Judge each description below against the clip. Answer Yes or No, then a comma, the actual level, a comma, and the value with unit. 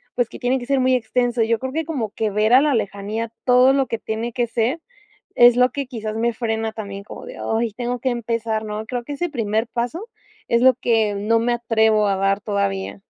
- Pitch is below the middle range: No, high, 230 Hz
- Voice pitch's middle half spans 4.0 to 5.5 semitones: No, narrow, 2.4 semitones